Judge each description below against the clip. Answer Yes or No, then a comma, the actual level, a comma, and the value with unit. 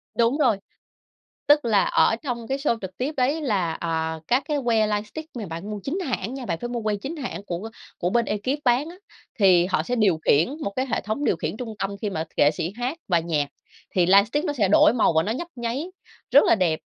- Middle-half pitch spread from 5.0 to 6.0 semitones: Yes, wide, 5.6 semitones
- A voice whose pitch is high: Yes, high, 225 Hz